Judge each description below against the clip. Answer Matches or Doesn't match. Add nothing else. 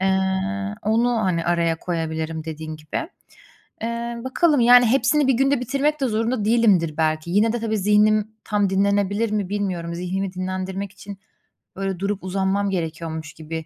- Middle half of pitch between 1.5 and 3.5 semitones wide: Doesn't match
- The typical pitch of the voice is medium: Doesn't match